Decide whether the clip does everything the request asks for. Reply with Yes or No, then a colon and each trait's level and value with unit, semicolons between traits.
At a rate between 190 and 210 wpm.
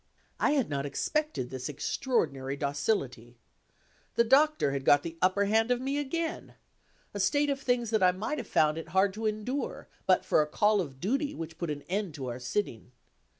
Yes: average, 195 wpm